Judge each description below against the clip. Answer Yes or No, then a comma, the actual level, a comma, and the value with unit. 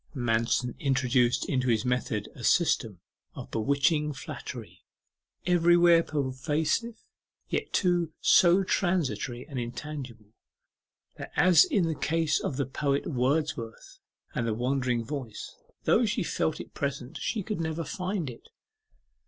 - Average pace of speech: No, slow, 130 wpm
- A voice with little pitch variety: No, average, 5.3 semitones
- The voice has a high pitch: No, medium, 140 Hz